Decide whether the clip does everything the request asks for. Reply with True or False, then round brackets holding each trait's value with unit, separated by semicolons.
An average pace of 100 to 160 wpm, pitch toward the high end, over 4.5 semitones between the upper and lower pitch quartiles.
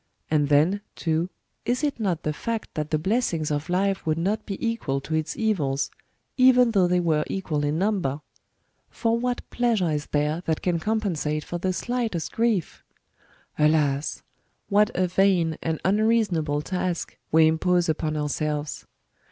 False (155 wpm; 175 Hz; 5.4 semitones)